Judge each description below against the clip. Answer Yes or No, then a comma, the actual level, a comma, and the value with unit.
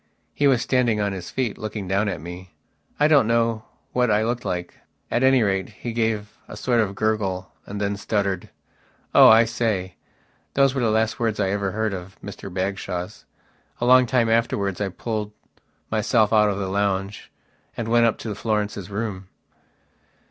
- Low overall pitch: Yes, low, 105 Hz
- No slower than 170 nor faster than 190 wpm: Yes, average, 175 wpm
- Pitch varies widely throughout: No, average, 2.9 semitones